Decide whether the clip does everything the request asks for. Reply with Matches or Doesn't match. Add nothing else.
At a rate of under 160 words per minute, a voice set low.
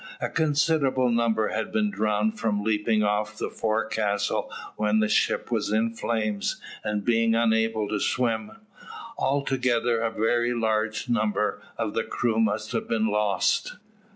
Matches